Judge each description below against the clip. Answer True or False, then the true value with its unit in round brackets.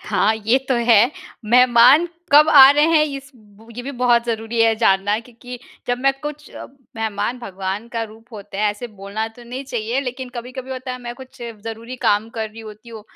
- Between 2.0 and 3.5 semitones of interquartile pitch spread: True (2.8 semitones)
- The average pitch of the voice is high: True (235 Hz)